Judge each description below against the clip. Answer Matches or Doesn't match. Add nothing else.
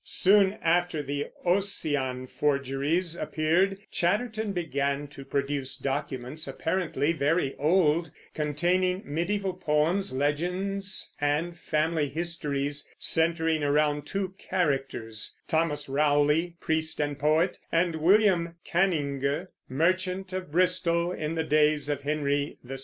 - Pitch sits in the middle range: Matches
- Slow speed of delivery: Matches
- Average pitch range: Matches